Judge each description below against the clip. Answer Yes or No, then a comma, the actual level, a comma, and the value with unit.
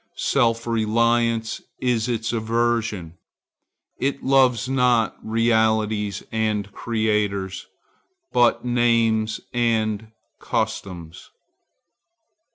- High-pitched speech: No, low, 115 Hz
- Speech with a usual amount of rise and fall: No, narrow, 1.7 semitones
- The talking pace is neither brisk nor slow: No, slow, 70 wpm